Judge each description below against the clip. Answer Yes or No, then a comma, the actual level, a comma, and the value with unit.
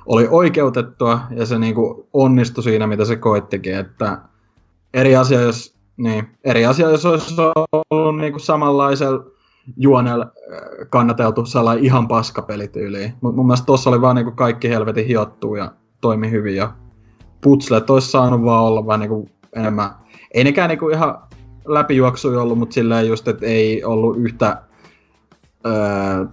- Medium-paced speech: Yes, average, 140 wpm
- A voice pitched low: Yes, low, 115 Hz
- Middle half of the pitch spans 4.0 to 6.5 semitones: No, average, 3.2 semitones